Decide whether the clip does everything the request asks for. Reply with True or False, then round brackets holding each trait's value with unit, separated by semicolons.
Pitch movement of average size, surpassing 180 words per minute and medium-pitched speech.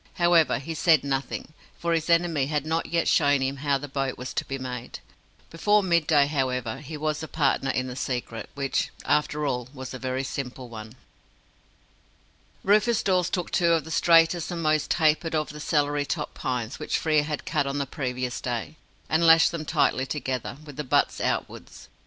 True (3.7 semitones; 190 wpm; 145 Hz)